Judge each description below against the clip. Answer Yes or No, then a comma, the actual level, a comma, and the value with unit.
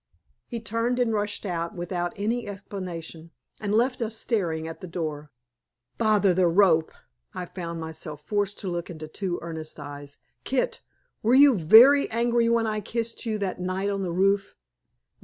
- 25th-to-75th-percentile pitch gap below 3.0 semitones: No, average, 4.9 semitones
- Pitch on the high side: Yes, high, 195 Hz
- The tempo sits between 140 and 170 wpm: Yes, average, 165 wpm